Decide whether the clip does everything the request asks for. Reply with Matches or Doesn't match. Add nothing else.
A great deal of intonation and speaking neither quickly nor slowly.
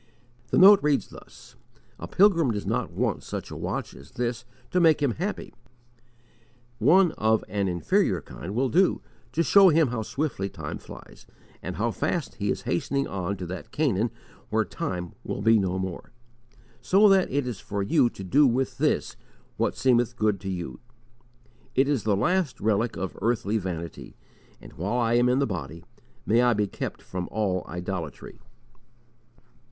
Matches